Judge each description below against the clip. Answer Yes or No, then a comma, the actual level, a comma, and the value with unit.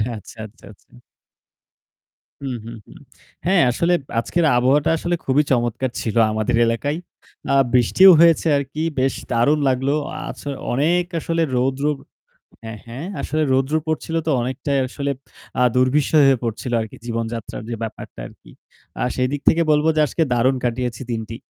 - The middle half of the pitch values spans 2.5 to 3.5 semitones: No, average, 4.1 semitones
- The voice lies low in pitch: Yes, low, 130 Hz